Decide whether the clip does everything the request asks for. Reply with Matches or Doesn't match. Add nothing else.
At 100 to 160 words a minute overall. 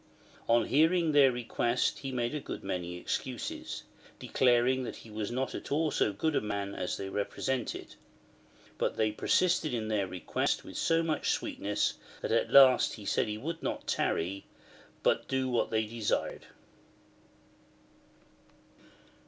Matches